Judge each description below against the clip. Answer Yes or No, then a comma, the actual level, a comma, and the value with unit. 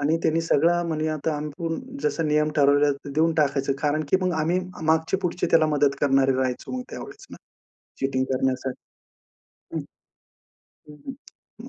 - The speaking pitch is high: No, medium, 150 Hz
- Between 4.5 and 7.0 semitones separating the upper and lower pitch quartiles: No, average, 2.8 semitones